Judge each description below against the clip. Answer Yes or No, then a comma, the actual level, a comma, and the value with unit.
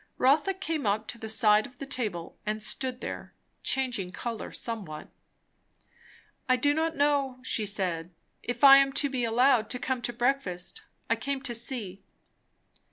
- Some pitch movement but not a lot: Yes, average, 4.3 semitones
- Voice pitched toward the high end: Yes, high, 245 Hz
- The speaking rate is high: No, average, 165 wpm